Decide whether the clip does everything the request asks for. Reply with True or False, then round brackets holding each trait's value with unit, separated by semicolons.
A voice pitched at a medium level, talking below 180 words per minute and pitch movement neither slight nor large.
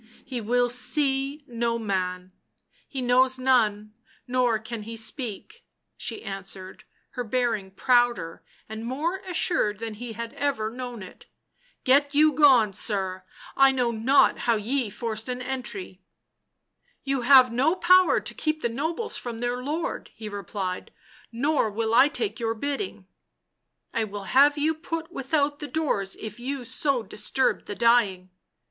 False (245 Hz; 160 wpm; 4.4 semitones)